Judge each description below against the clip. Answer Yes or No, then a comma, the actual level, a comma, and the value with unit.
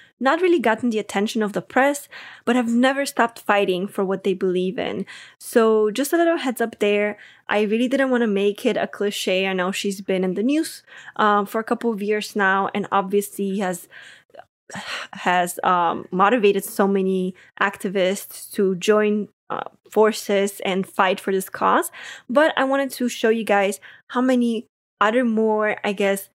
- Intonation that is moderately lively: Yes, average, 3.3 semitones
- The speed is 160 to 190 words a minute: Yes, average, 180 wpm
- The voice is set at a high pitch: Yes, high, 210 Hz